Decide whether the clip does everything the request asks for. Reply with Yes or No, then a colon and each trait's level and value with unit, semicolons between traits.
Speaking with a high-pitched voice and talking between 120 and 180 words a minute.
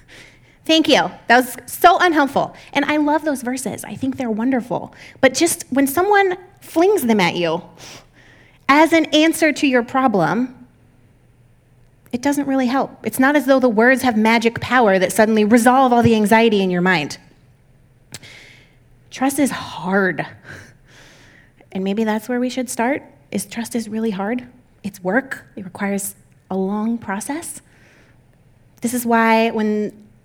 Yes: high, 225 Hz; average, 155 wpm